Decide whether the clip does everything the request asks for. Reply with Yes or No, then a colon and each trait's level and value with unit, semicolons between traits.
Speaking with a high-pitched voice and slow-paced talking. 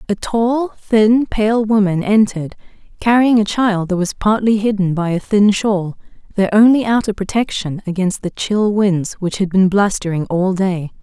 No: high, 200 Hz; average, 170 wpm